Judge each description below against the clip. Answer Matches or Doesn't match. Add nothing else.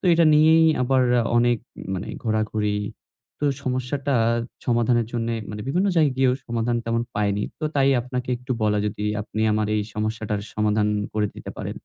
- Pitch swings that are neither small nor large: Matches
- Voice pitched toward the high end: Doesn't match